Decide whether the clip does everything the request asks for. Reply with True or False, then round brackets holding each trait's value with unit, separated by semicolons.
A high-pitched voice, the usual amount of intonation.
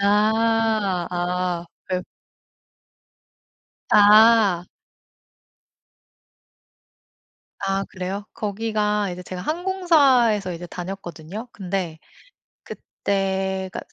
True (195 Hz; 3.2 semitones)